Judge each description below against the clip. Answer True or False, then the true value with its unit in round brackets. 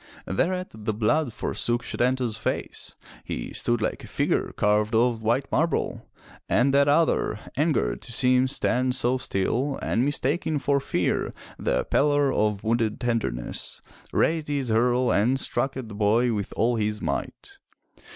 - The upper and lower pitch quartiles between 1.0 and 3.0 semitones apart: False (4.1 semitones)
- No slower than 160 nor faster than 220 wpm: False (150 wpm)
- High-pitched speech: False (125 Hz)